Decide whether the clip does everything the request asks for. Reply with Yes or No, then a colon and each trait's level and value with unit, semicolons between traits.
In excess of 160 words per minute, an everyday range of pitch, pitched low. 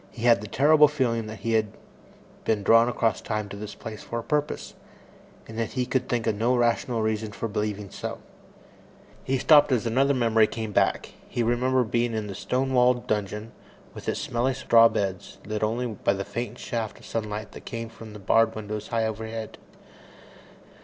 No: average, 190 wpm; narrow, 2.2 semitones; low, 115 Hz